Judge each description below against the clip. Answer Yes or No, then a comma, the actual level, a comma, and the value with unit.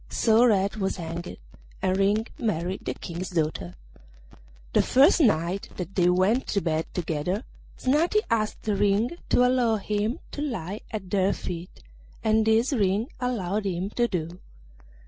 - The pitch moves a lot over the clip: No, average, 4.1 semitones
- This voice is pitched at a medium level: No, high, 200 Hz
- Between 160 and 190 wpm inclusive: No, average, 145 wpm